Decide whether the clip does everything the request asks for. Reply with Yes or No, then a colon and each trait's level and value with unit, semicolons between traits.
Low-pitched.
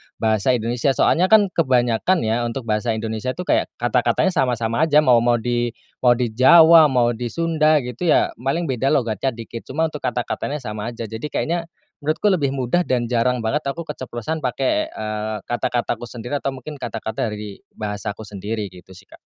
Yes: low, 125 Hz